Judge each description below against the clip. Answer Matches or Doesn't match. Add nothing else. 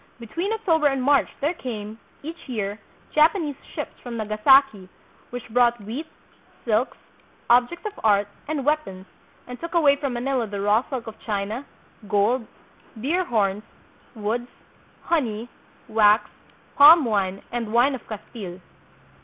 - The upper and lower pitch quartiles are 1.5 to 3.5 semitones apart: Doesn't match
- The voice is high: Matches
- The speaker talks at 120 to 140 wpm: Matches